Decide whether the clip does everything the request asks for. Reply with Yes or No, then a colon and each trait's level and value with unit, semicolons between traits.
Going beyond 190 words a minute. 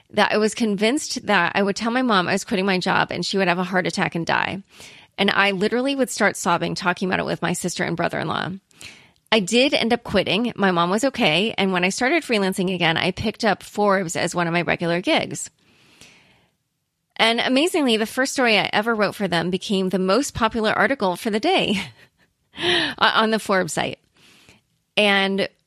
Yes: average, 200 wpm